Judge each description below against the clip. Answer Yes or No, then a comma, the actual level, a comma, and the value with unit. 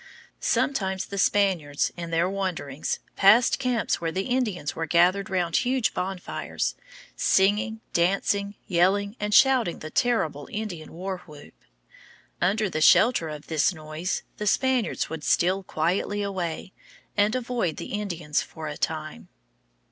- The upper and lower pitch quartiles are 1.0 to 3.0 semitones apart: No, average, 4.1 semitones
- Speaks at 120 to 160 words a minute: Yes, slow, 135 wpm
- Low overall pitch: No, high, 190 Hz